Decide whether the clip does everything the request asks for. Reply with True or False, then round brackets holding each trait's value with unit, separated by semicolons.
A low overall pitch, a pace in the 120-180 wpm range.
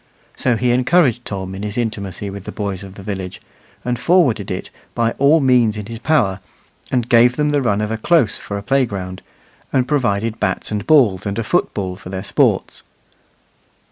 False (110 Hz; 190 wpm)